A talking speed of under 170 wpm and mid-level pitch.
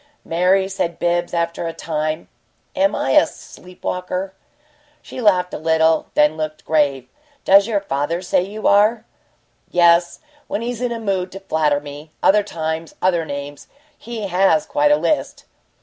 Yes: average, 160 wpm; medium, 180 Hz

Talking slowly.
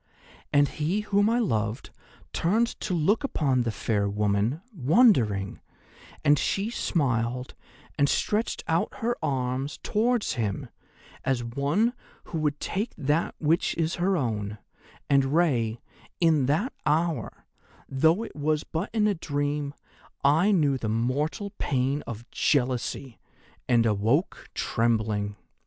Yes: slow, 130 wpm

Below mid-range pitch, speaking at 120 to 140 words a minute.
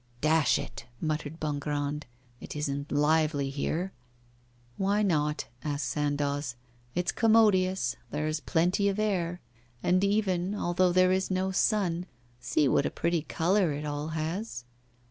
No: medium, 160 Hz; slow, 135 wpm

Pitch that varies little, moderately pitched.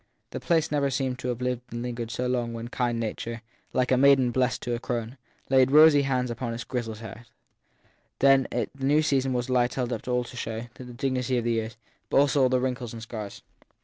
No: narrow, 2.0 semitones; low, 125 Hz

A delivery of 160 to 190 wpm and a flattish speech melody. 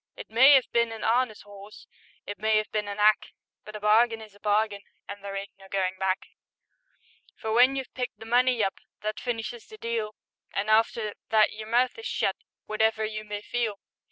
No: average, 200 wpm; narrow, 2.1 semitones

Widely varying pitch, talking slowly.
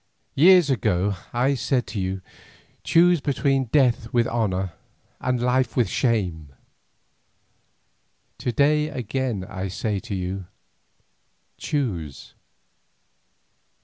Yes: wide, 5.8 semitones; slow, 100 wpm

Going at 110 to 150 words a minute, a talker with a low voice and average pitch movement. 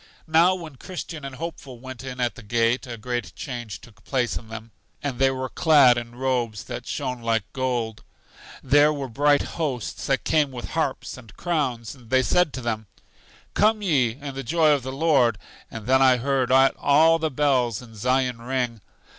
No: average, 190 wpm; low, 130 Hz; average, 3.4 semitones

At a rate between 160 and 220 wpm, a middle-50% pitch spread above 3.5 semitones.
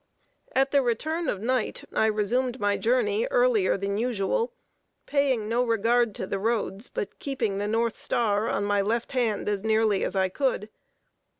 Yes: average, 170 wpm; average, 4.3 semitones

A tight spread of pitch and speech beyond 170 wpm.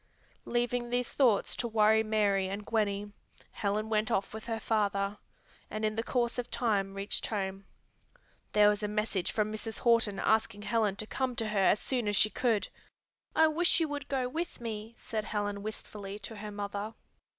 Yes: narrow, 2.3 semitones; average, 185 wpm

